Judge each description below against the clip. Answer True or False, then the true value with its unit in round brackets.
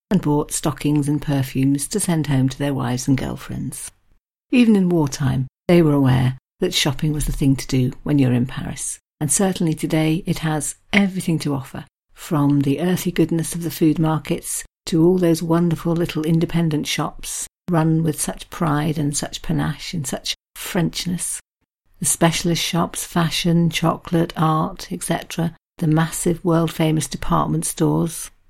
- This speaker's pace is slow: False (160 wpm)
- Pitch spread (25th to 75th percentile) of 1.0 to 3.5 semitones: True (2.5 semitones)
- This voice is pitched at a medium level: True (160 Hz)